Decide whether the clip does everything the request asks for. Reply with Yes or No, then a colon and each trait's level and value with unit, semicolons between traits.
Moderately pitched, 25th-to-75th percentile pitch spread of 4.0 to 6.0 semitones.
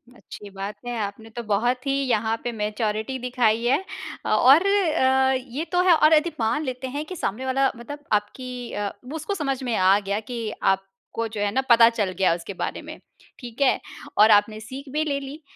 No: high, 240 Hz; average, 4.5 semitones